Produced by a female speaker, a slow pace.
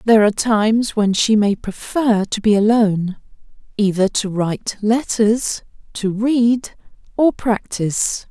Yes: female; slow, 130 wpm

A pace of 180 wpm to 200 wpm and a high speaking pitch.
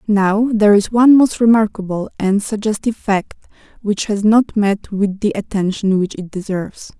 No: average, 165 wpm; high, 205 Hz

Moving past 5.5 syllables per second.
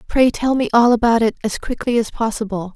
Yes: 5.7 syllables/s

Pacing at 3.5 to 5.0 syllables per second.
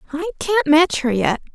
Yes: 4.6 syllables/s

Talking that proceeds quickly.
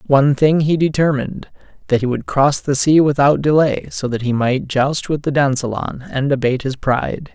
No: average, 195 wpm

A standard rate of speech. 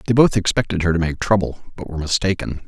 No: fast, 225 wpm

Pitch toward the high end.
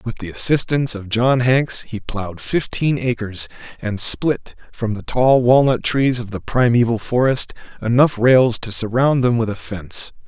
No: low, 120 Hz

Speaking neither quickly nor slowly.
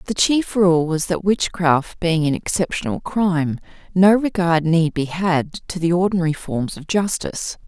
Yes: average, 165 wpm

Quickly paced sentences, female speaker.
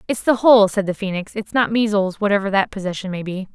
Yes: fast, 235 wpm; female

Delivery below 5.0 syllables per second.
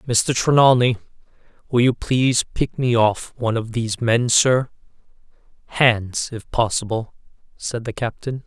Yes: 4.4 syllables/s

